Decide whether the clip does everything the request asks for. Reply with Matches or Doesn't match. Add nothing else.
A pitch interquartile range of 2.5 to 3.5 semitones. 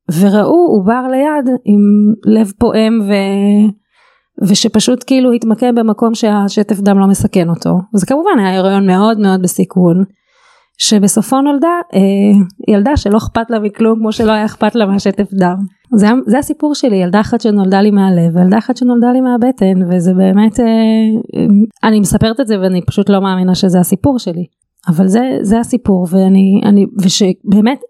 Matches